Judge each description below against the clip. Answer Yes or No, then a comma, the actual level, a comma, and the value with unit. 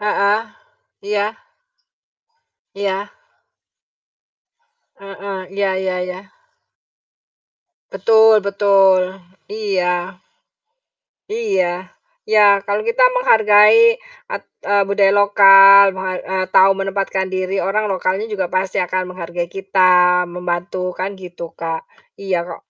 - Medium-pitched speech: No, high, 195 Hz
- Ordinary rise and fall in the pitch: No, narrow, 1.7 semitones